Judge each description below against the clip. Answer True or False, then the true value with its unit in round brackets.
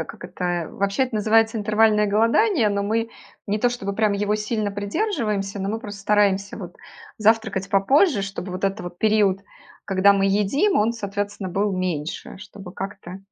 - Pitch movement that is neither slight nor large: False (2.0 semitones)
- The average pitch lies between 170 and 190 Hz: False (205 Hz)